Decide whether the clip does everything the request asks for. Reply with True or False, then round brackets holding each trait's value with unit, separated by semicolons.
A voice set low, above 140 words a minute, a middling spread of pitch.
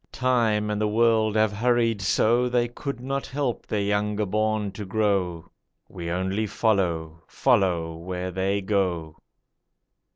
False (105 Hz; 135 wpm; 3.5 semitones)